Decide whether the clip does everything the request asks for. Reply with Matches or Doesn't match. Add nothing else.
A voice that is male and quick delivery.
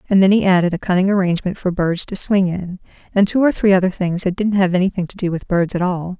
Doesn't match